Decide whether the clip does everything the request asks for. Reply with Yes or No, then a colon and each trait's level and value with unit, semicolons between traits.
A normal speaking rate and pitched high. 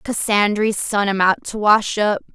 Yes: average, 180 wpm; high, 205 Hz